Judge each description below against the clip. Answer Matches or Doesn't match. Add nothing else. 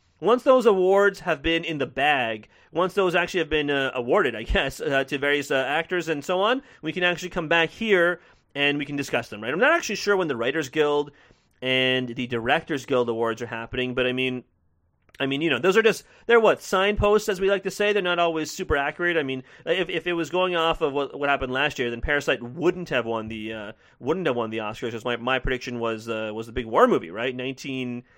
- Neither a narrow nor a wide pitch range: Doesn't match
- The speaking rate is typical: Doesn't match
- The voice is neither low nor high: Matches